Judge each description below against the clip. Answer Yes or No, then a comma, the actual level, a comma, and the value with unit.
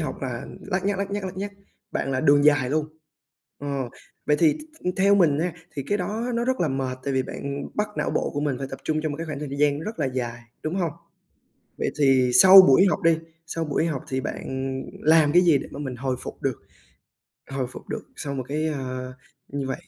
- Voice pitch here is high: No, medium, 150 Hz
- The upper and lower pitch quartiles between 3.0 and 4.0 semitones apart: No, average, 4.7 semitones